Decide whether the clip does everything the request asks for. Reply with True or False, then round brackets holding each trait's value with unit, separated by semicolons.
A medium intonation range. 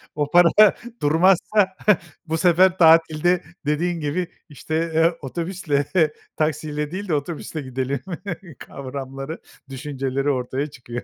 True (3.6 semitones)